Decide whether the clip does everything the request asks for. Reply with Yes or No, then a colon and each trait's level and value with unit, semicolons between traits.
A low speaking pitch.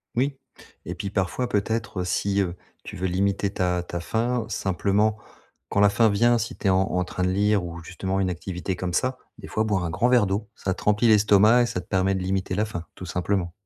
Yes: low, 100 Hz